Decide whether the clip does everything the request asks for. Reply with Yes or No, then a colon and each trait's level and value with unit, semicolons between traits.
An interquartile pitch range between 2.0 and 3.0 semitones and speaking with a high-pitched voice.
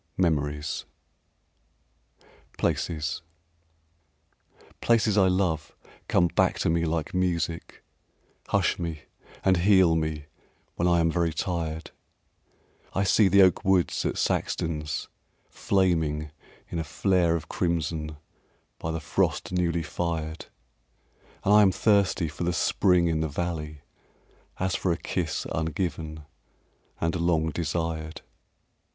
No: narrow, 2.4 semitones; very low, 85 Hz